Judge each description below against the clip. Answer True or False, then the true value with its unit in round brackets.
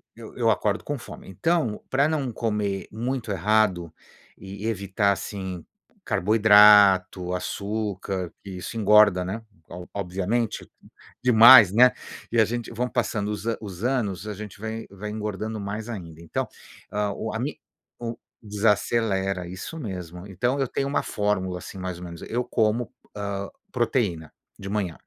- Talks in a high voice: False (105 Hz)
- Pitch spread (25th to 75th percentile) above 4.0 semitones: False (3.0 semitones)